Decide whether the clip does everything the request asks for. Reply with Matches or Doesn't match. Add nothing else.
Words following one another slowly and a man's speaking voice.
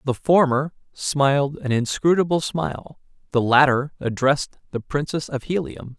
Matches